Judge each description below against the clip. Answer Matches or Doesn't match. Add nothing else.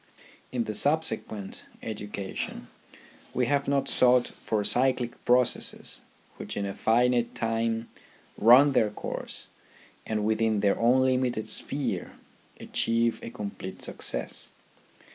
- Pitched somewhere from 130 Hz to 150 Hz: Doesn't match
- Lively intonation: Doesn't match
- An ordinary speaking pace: Doesn't match